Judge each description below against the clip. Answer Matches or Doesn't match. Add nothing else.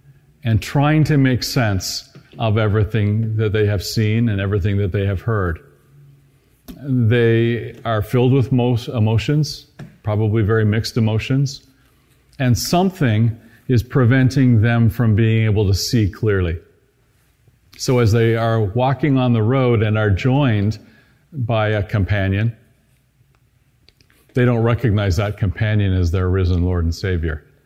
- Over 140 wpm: Doesn't match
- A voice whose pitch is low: Matches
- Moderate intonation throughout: Matches